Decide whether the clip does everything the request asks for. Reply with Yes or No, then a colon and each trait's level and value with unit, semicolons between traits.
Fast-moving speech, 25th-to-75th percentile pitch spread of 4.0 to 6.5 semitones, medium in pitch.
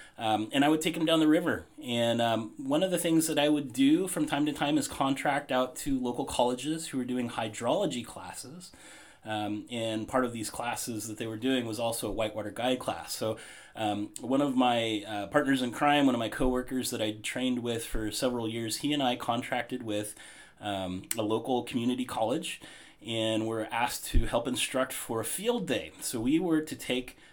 No: fast, 210 wpm; average, 4.5 semitones; low, 125 Hz